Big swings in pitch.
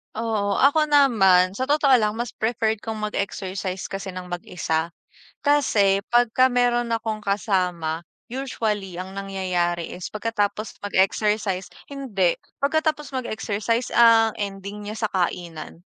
No: average, 3.9 semitones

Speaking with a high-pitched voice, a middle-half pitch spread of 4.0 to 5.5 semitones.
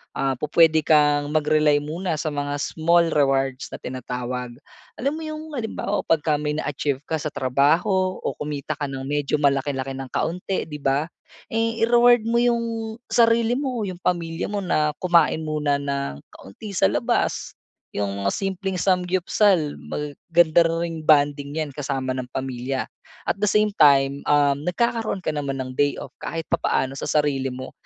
No: medium, 150 Hz; average, 5.0 semitones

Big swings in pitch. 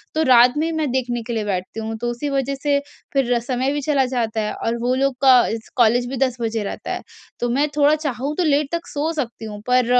No: average, 3.3 semitones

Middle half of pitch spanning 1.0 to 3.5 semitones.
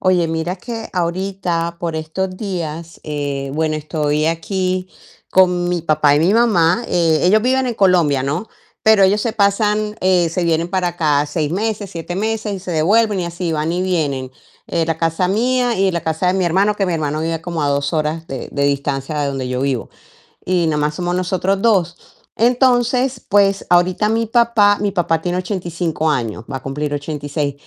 No: average, 4.2 semitones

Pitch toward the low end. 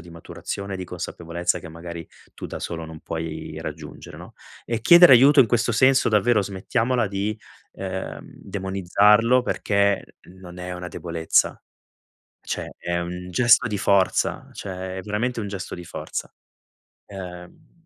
Yes: very low, 95 Hz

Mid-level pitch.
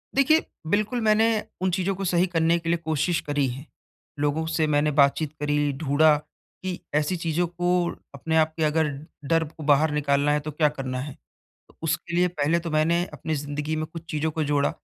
Yes: medium, 155 Hz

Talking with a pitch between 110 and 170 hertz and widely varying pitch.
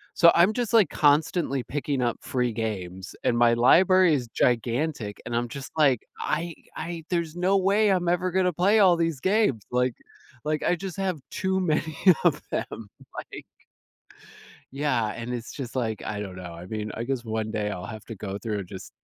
Yes: low, 135 Hz; wide, 7.7 semitones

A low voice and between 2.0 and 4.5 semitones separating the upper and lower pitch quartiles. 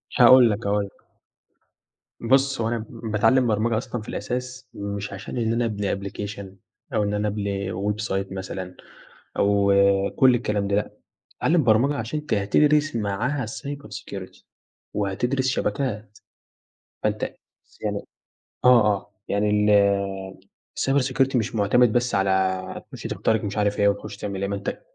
Yes: low, 105 Hz; average, 3.5 semitones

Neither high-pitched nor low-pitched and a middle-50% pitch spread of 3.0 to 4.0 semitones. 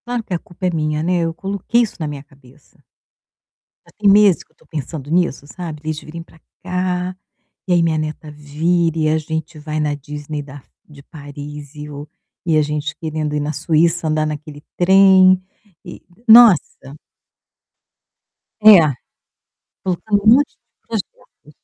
Yes: medium, 155 Hz; average, 3.4 semitones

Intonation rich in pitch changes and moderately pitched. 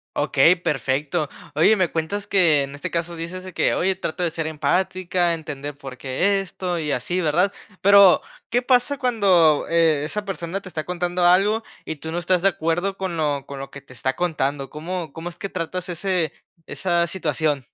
No: average, 3.5 semitones; medium, 170 Hz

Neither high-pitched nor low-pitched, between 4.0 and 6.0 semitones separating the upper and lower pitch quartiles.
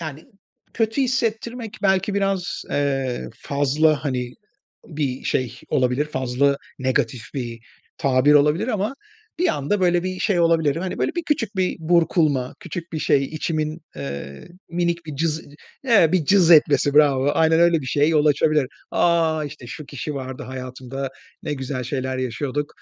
Yes: medium, 150 Hz; average, 4.5 semitones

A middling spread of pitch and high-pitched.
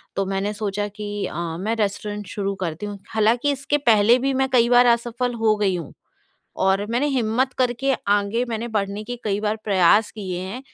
Yes: average, 3.2 semitones; high, 210 Hz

